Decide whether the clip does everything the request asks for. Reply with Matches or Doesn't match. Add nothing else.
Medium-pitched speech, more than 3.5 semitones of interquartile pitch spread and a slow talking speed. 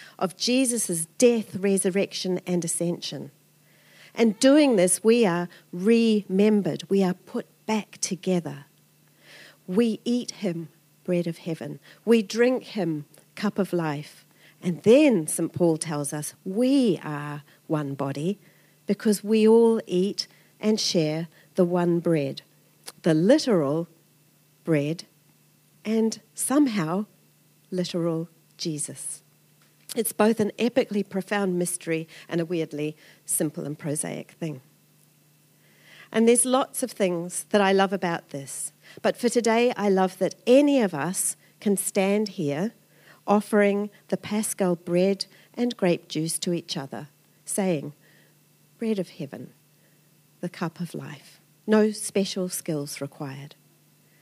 Matches